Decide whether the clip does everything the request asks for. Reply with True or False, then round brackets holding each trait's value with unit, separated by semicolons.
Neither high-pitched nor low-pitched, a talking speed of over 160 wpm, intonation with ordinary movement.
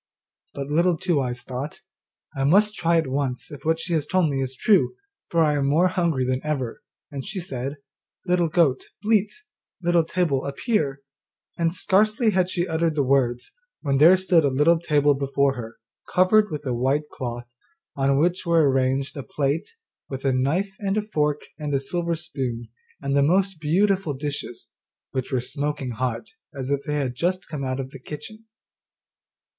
True (150 Hz; 180 wpm; 4.5 semitones)